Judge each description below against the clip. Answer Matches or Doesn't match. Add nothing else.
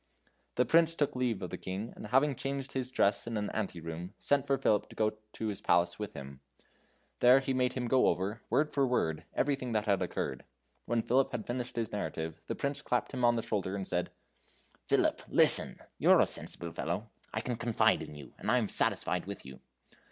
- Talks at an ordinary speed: Doesn't match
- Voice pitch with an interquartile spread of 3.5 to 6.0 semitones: Matches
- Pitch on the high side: Doesn't match